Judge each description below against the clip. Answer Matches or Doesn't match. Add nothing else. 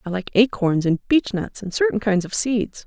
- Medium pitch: Doesn't match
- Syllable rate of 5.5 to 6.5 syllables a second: Doesn't match